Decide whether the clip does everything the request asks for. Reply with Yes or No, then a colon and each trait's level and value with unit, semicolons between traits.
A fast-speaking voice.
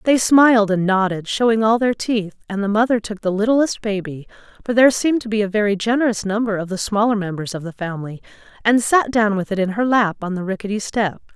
Yes: fast, 225 wpm